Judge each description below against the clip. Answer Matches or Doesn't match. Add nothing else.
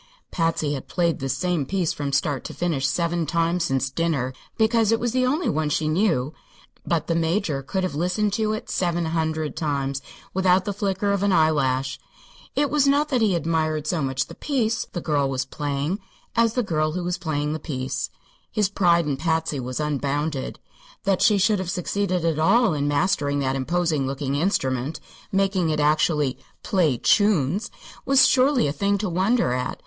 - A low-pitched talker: Doesn't match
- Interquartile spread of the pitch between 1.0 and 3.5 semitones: Doesn't match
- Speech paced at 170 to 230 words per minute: Matches